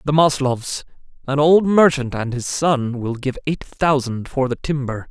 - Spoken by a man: Yes, male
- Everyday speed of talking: Yes, average, 175 wpm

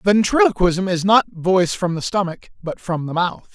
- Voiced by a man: Yes, male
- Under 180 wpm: No, average, 185 wpm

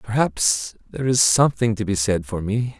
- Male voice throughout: Yes, male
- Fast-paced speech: No, average, 195 wpm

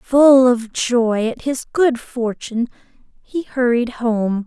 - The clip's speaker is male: No, female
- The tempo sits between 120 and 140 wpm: Yes, slow, 135 wpm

